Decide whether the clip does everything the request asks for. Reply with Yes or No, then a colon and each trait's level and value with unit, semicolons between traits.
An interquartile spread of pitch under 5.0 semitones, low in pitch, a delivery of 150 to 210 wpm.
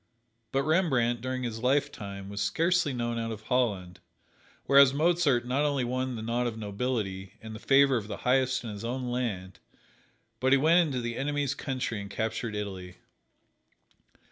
Yes: average, 3.8 semitones; low, 125 Hz; average, 170 wpm